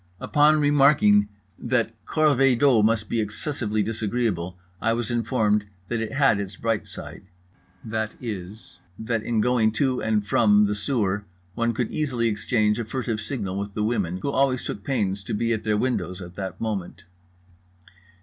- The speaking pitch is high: No, low, 110 Hz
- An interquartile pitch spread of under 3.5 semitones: Yes, average, 3.1 semitones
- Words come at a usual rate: Yes, average, 160 wpm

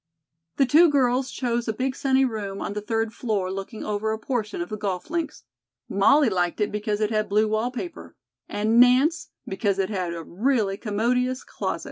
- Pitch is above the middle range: Yes, high, 220 Hz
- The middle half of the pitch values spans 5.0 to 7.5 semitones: No, average, 3.8 semitones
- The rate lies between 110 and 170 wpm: No, average, 185 wpm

